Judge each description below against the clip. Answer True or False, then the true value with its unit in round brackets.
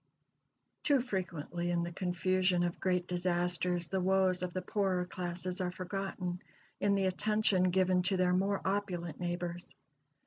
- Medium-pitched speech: True (180 Hz)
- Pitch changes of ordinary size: False (1.3 semitones)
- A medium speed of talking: True (145 wpm)